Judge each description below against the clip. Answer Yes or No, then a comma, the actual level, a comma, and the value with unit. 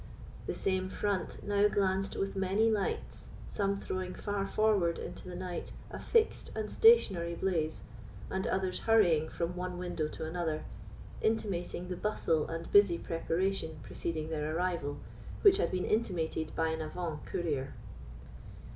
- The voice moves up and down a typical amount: Yes, average, 3.3 semitones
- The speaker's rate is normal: Yes, average, 145 wpm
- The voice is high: No, medium, 180 Hz